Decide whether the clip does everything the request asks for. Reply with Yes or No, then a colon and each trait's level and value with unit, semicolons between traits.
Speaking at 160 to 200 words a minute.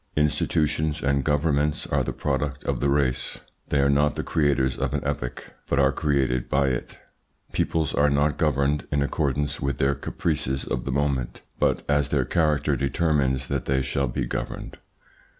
Yes: average, 170 wpm